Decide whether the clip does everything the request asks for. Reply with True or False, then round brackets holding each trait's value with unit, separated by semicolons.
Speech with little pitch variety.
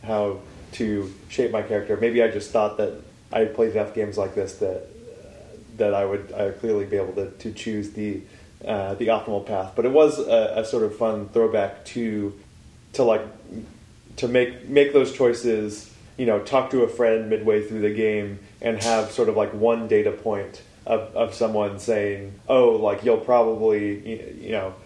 True (2.2 semitones)